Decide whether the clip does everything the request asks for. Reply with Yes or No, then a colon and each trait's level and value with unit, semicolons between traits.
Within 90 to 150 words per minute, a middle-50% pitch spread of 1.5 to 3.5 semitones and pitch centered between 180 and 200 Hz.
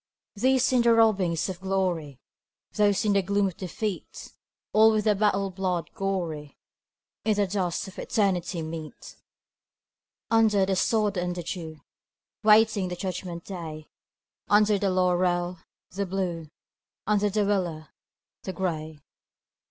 Yes: slow, 135 wpm; average, 2.9 semitones; high, 190 Hz